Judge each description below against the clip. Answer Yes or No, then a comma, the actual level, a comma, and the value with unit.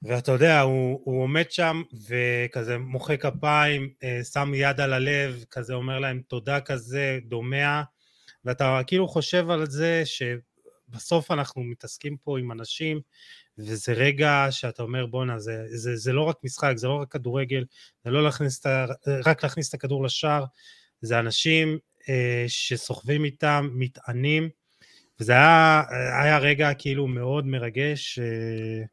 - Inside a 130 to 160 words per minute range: Yes, average, 145 wpm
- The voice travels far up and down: No, average, 3.1 semitones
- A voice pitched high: No, low, 135 Hz